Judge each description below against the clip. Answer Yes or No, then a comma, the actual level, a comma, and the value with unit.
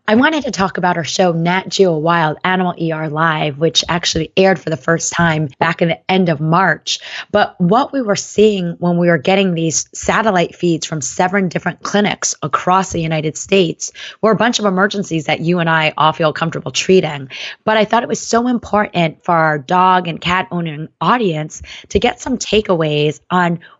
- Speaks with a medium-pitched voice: Yes, medium, 175 Hz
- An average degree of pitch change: Yes, average, 3.5 semitones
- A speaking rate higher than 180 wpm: Yes, average, 195 wpm